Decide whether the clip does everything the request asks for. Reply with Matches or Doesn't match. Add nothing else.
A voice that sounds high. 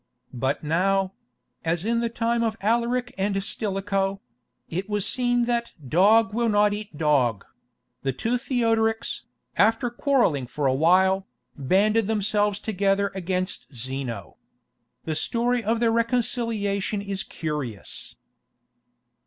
Matches